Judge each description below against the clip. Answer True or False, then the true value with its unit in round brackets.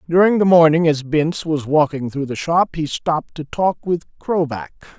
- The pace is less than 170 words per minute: False (195 wpm)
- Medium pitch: True (160 Hz)